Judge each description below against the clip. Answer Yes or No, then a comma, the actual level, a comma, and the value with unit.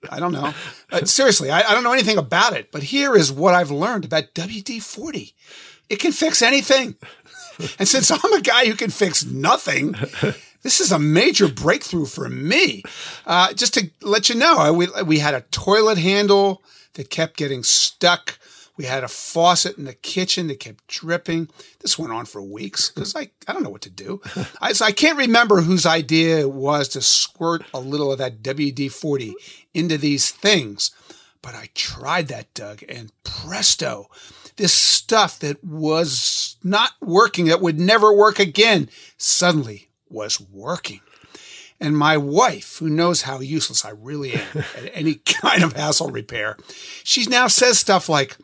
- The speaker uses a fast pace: No, average, 175 wpm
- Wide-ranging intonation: Yes, wide, 6.2 semitones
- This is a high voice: No, medium, 170 Hz